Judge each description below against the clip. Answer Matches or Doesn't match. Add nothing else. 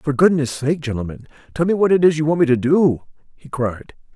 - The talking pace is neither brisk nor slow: Doesn't match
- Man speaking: Matches